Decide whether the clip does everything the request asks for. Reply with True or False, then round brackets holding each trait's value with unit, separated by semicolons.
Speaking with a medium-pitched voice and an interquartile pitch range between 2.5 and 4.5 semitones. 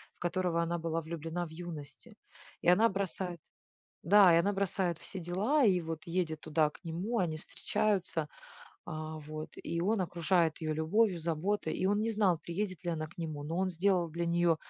True (170 Hz; 3.0 semitones)